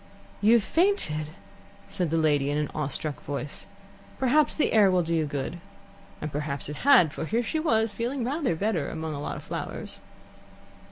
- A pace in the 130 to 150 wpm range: No, average, 185 wpm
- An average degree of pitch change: No, wide, 7.6 semitones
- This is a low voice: No, medium, 165 Hz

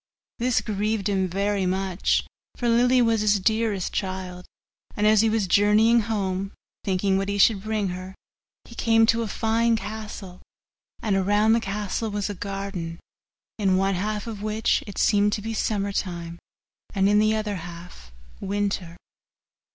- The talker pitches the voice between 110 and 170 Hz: No, high, 205 Hz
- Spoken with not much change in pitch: Yes, narrow, 2.3 semitones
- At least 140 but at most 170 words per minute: Yes, average, 160 wpm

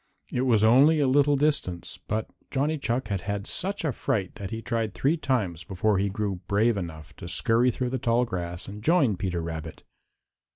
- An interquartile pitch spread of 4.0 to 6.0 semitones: Yes, wide, 5.6 semitones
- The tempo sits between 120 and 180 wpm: No, average, 195 wpm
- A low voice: Yes, low, 110 Hz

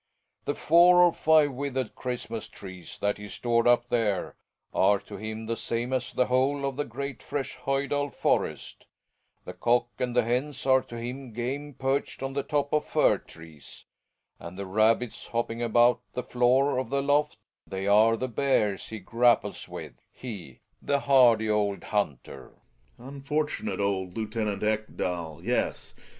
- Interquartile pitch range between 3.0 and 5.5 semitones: Yes, average, 4.3 semitones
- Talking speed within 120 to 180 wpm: Yes, average, 160 wpm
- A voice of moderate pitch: No, low, 120 Hz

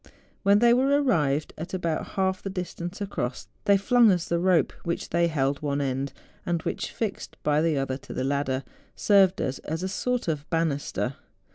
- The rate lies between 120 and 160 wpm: No, average, 185 wpm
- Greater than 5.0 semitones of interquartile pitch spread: Yes, wide, 5.5 semitones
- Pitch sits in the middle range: Yes, medium, 170 Hz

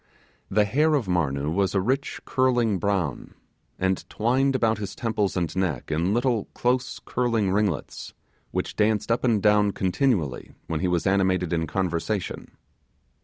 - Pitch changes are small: No, average, 4.5 semitones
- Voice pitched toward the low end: Yes, low, 100 Hz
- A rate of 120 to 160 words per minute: Yes, average, 150 wpm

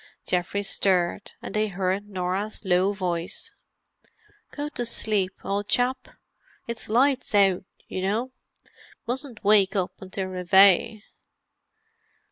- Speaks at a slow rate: Yes, slow, 115 wpm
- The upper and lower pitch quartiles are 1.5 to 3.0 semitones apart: Yes, average, 2.7 semitones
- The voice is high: Yes, high, 200 Hz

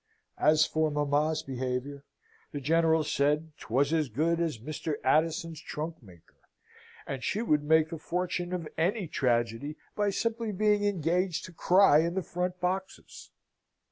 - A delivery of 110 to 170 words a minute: Yes, average, 145 wpm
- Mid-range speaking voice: Yes, medium, 160 Hz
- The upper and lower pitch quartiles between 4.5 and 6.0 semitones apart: No, average, 3.5 semitones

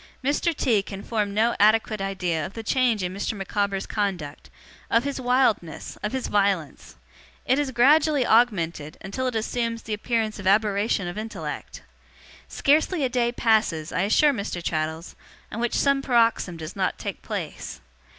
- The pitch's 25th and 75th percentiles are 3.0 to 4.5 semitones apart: Yes, average, 4.1 semitones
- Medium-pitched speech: No, high, 215 Hz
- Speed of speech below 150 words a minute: No, average, 160 wpm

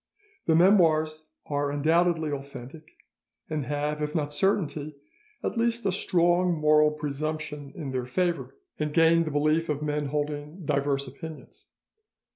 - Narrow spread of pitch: Yes, narrow, 2.2 semitones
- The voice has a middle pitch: Yes, medium, 150 Hz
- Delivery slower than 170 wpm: Yes, slow, 135 wpm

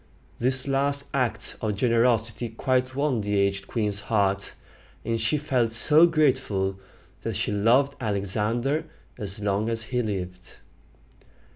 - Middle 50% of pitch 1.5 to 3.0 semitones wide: No, average, 4.2 semitones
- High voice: No, low, 115 Hz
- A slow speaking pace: Yes, slow, 130 wpm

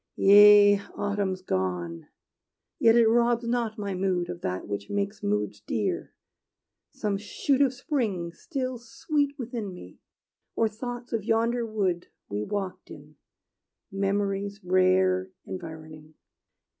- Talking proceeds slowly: Yes, slow, 120 wpm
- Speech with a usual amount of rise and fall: Yes, average, 4.7 semitones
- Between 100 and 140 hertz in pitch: No, high, 200 Hz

